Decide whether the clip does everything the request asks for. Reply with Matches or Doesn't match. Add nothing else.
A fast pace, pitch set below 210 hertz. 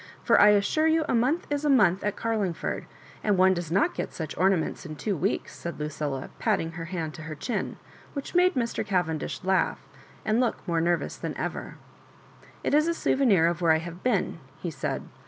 Matches